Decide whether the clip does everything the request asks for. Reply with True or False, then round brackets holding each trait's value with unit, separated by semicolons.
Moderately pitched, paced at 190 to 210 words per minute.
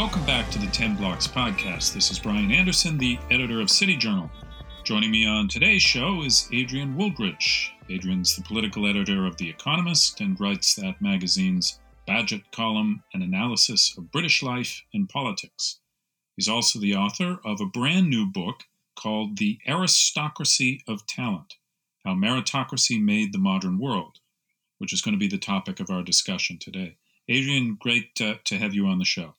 False (155 Hz; 170 wpm)